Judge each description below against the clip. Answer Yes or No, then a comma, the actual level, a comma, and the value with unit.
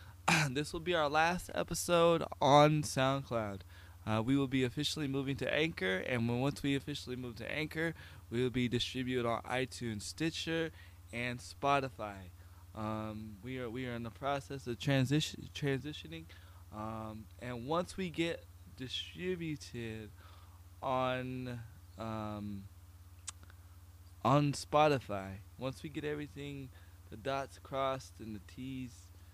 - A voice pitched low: Yes, low, 120 Hz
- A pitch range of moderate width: No, wide, 6.8 semitones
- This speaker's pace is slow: Yes, slow, 130 wpm